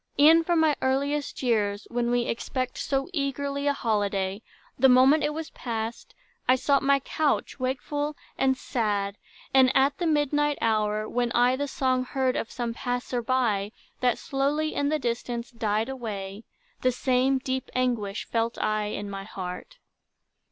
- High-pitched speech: Yes, very high, 255 Hz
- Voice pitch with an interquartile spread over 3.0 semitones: Yes, average, 3.7 semitones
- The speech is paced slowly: No, average, 160 wpm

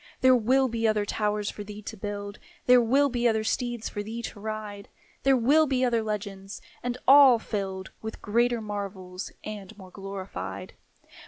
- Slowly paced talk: No, average, 170 wpm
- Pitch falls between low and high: No, high, 215 Hz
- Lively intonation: No, average, 3.0 semitones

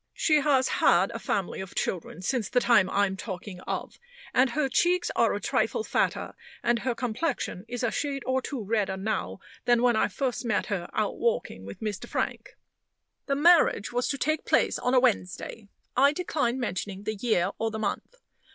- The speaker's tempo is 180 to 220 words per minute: Yes, average, 190 wpm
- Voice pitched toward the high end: Yes, high, 235 Hz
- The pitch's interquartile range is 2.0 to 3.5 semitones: No, average, 4.8 semitones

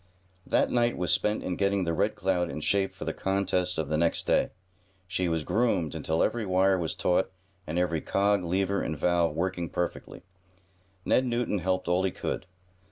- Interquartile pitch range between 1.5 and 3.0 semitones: Yes, narrow, 2.4 semitones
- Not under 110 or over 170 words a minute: No, average, 185 wpm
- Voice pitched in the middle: No, very low, 90 Hz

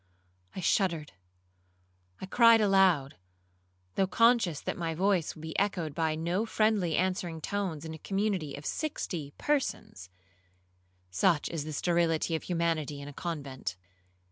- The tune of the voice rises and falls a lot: Yes, wide, 6.0 semitones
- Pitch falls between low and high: Yes, medium, 160 Hz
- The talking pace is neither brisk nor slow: No, slow, 130 wpm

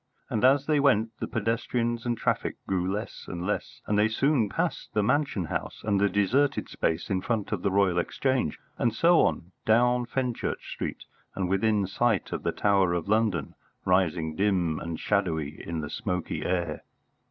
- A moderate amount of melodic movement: Yes, average, 4.7 semitones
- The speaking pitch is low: Yes, low, 100 Hz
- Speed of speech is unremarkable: Yes, average, 175 wpm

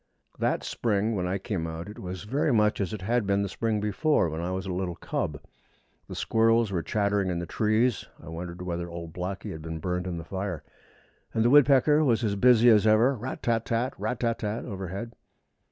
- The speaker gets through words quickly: Yes, fast, 220 wpm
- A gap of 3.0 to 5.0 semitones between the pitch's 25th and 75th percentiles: Yes, average, 4.3 semitones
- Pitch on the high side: No, low, 100 Hz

